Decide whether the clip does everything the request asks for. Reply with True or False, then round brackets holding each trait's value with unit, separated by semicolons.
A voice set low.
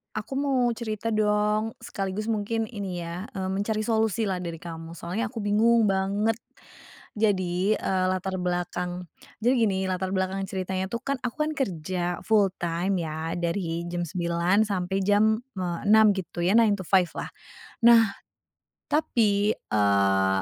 False (195 Hz)